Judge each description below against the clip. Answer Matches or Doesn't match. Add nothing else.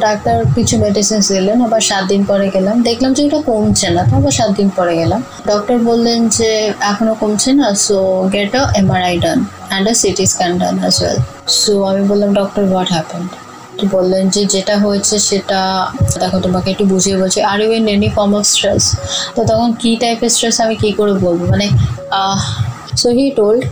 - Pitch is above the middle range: Matches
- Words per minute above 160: Matches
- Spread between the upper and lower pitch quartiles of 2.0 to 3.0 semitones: Matches